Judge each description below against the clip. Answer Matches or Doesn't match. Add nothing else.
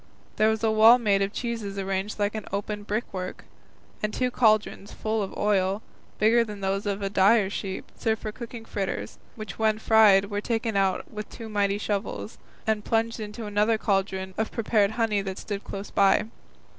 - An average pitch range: Doesn't match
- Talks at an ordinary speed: Matches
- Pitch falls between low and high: Doesn't match